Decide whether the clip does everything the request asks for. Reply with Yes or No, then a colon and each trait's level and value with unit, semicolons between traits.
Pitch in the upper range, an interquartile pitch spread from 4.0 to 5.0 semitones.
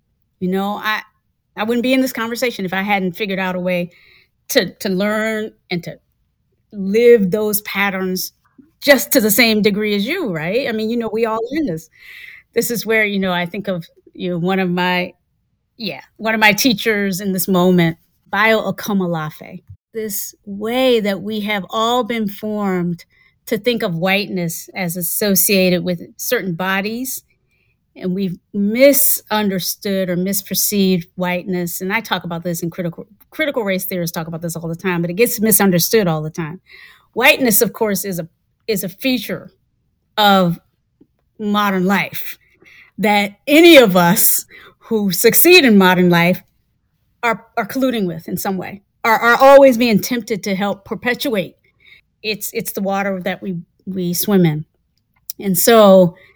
No: high, 200 Hz; average, 3.6 semitones